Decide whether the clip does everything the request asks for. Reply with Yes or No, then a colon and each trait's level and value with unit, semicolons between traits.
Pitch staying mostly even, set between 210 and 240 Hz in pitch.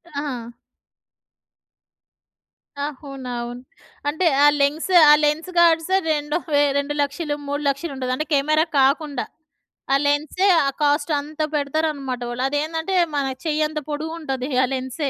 No: narrow, 2.2 semitones; very high, 290 Hz